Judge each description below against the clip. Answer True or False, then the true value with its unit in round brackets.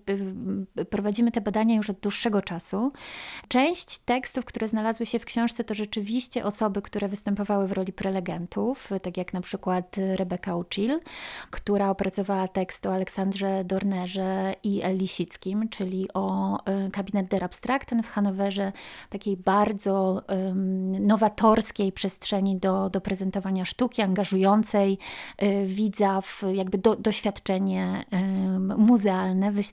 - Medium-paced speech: True (125 wpm)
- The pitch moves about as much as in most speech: False (2.1 semitones)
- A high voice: True (200 Hz)